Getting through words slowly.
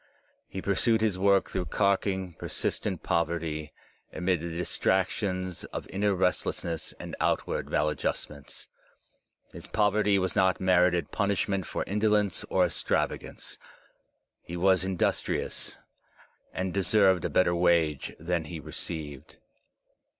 Yes: slow, 120 wpm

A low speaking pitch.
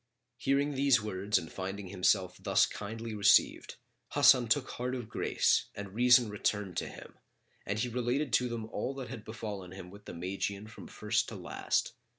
Yes: low, 110 Hz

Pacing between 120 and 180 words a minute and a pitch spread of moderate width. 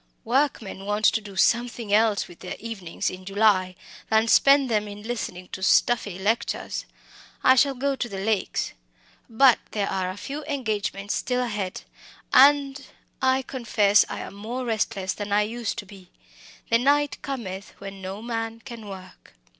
Yes: average, 160 wpm; average, 3.8 semitones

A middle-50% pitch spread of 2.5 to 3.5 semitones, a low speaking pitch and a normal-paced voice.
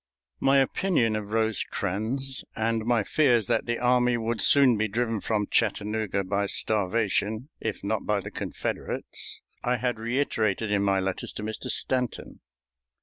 Yes: average, 2.8 semitones; low, 110 Hz; average, 145 wpm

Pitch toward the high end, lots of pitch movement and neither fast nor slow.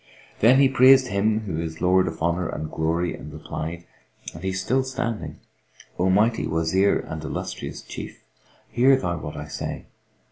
No: very low, 95 Hz; wide, 6.0 semitones; average, 170 wpm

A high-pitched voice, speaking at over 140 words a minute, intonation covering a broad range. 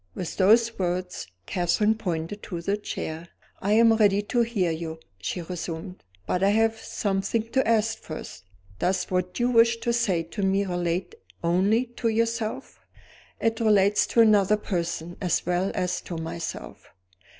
No: high, 195 Hz; average, 155 wpm; average, 4.1 semitones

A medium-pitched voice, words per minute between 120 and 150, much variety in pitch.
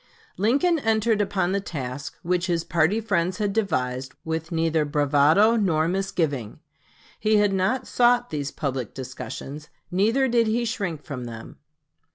Yes: medium, 180 Hz; average, 145 wpm; wide, 6.6 semitones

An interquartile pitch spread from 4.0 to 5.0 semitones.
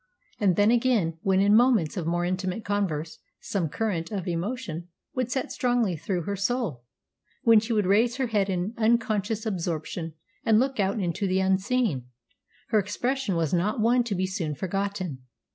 Yes: average, 4.4 semitones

